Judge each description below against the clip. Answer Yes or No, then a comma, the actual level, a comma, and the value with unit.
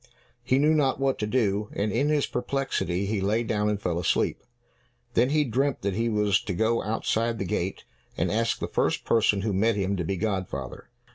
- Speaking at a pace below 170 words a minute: No, fast, 205 wpm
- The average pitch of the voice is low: Yes, low, 110 Hz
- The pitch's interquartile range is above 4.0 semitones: No, average, 3.7 semitones